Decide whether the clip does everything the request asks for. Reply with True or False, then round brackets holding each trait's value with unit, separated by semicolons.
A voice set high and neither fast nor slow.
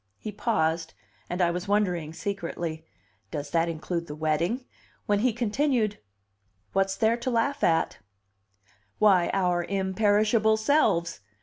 False (195 Hz; 125 wpm)